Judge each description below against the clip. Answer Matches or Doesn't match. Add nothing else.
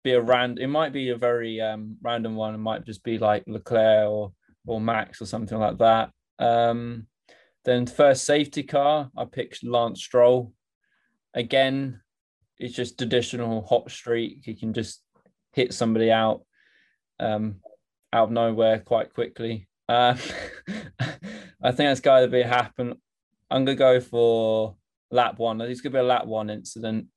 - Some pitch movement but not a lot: Doesn't match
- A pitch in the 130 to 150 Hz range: Doesn't match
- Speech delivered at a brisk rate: Doesn't match